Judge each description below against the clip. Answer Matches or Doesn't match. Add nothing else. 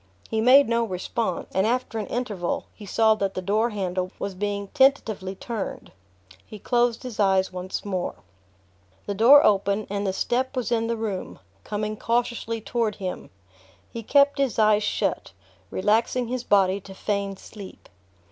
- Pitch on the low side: Doesn't match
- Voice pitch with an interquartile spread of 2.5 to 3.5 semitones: Matches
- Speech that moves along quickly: Doesn't match